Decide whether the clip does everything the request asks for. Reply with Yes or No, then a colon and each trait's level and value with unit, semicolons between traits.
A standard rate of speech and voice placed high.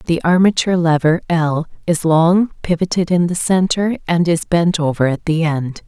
No: average, 175 wpm; medium, 170 Hz